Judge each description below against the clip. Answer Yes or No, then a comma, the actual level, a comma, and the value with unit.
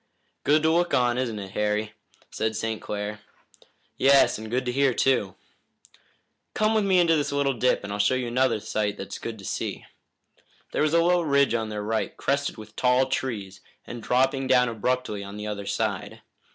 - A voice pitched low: Yes, low, 125 Hz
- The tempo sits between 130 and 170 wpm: No, average, 190 wpm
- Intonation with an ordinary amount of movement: Yes, average, 4.5 semitones